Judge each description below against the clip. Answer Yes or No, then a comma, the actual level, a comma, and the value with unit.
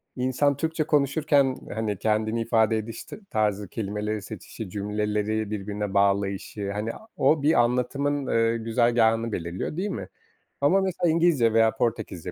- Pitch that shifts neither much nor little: Yes, average, 4.9 semitones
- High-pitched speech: No, low, 115 Hz